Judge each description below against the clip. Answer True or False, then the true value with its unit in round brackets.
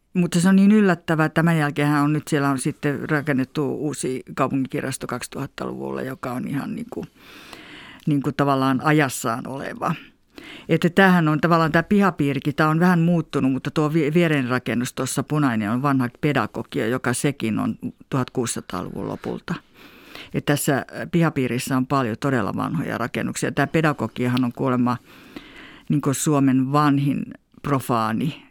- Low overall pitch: False (145 Hz)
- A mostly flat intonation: False (3.9 semitones)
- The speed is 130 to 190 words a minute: True (140 wpm)